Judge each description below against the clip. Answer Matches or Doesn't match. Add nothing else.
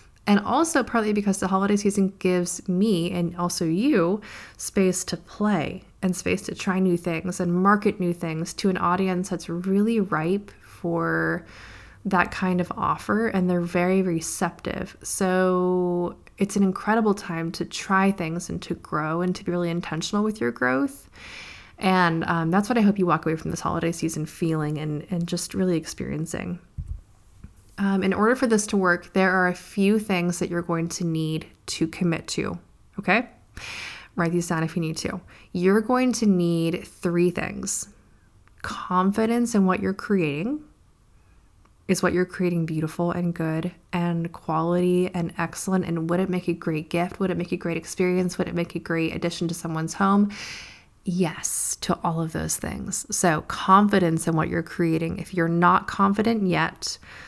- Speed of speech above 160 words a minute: Matches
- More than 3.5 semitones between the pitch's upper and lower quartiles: Doesn't match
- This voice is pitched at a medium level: Matches